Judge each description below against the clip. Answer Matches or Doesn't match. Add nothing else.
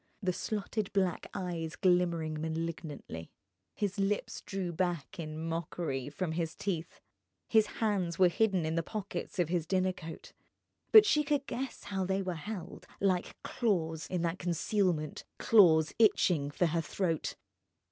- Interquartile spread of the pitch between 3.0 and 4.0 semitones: Matches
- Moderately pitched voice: Matches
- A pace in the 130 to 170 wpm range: Matches